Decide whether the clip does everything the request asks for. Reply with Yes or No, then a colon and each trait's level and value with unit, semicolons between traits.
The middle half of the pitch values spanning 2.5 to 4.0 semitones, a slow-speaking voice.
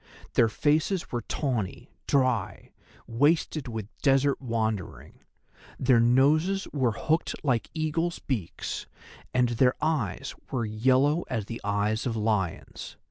No: average, 4.8 semitones; slow, 120 wpm